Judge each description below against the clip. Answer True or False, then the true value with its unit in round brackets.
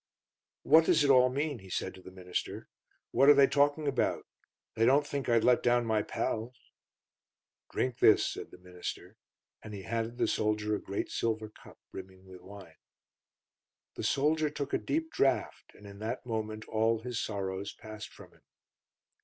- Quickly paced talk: False (175 wpm)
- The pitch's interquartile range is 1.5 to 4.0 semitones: False (5.1 semitones)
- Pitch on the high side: False (115 Hz)